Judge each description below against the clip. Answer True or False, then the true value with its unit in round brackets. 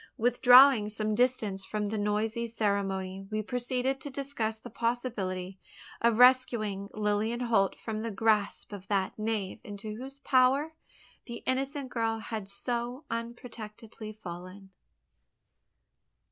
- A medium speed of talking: False (120 wpm)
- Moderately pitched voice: False (220 Hz)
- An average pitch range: True (3.1 semitones)